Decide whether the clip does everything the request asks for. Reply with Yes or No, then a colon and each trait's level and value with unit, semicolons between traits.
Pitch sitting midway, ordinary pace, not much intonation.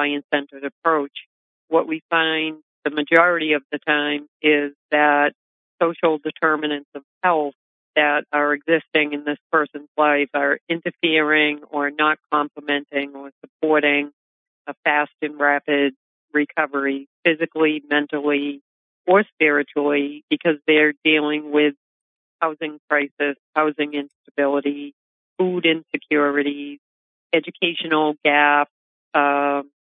No: medium, 150 Hz; slow, 105 wpm; narrow, 1.3 semitones